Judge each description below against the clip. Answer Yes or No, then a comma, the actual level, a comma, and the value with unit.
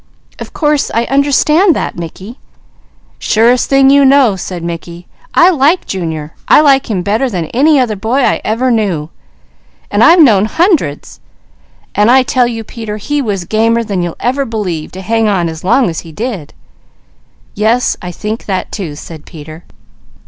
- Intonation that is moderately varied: No, wide, 6.8 semitones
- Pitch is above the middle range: Yes, high, 220 Hz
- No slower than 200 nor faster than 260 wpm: No, average, 165 wpm